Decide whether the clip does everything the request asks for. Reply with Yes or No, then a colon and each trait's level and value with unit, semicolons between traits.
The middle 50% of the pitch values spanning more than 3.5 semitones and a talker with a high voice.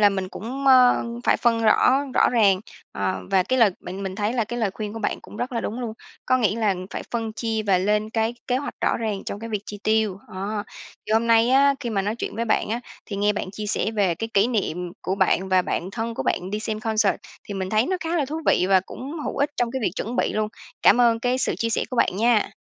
No: average, 3.1 semitones; high, 220 Hz